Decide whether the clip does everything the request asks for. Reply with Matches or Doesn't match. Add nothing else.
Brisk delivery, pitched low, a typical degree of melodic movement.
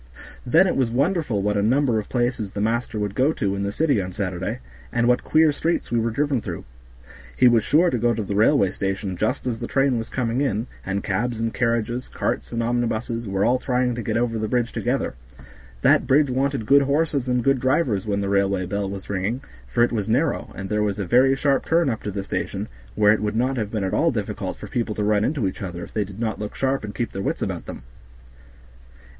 Matches